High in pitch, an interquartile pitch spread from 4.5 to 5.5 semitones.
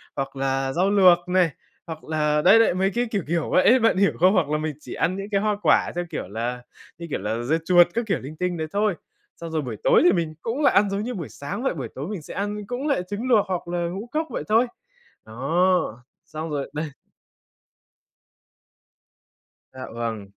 No: medium, 175 Hz; average, 5.2 semitones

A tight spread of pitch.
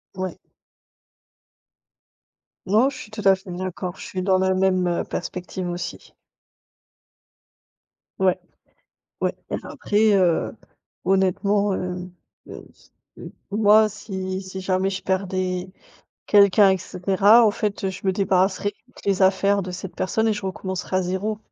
Yes: narrow, 1.5 semitones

